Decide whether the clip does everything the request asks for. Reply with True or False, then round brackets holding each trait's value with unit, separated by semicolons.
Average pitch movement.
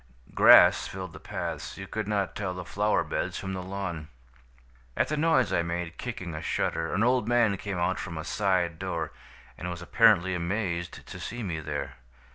True (3.5 semitones)